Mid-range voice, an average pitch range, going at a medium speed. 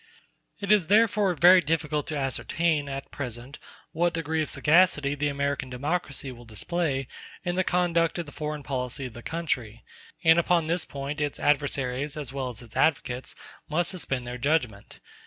Yes: medium, 145 Hz; average, 4.0 semitones; average, 170 wpm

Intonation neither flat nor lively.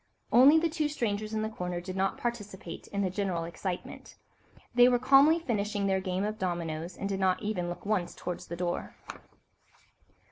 Yes: average, 4.5 semitones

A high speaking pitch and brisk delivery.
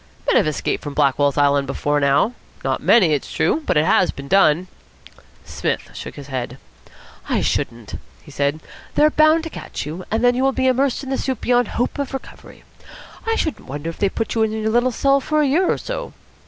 Yes: high, 220 Hz; fast, 215 wpm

